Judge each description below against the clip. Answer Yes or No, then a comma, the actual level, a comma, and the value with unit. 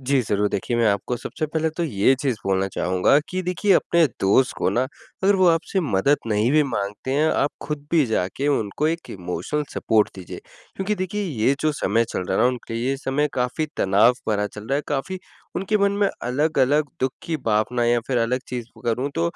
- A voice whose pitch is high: No, low, 130 Hz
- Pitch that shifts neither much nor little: No, wide, 6.2 semitones